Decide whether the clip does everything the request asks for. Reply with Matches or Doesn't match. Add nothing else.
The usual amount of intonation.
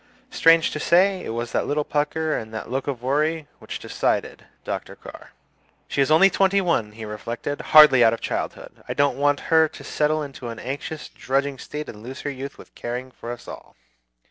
Matches